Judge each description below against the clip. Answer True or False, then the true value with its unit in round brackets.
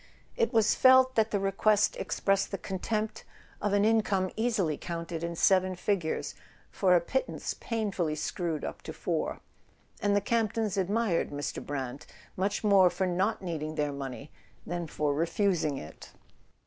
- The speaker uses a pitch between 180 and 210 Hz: True (190 Hz)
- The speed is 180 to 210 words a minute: False (155 wpm)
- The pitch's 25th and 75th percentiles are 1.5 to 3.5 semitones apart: False (4.2 semitones)